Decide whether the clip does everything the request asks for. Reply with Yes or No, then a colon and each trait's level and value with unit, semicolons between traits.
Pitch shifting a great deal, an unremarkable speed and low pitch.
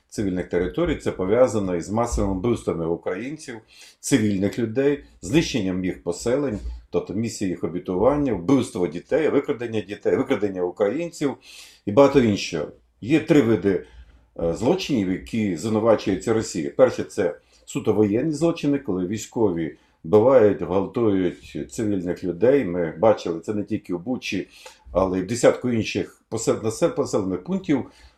Yes: wide, 7.0 semitones; average, 125 wpm; low, 110 Hz